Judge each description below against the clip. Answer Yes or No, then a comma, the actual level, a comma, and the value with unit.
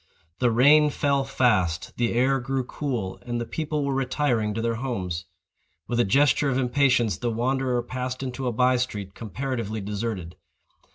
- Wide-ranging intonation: No, average, 3.1 semitones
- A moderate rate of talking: Yes, average, 165 wpm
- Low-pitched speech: Yes, low, 125 Hz